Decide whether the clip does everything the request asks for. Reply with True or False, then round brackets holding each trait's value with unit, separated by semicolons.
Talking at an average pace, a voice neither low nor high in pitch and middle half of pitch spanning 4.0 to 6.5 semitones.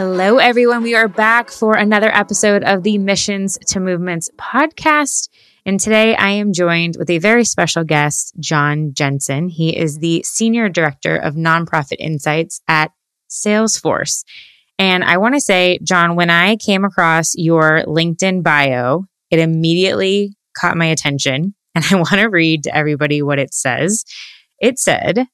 True (155 wpm; 180 Hz; 4.4 semitones)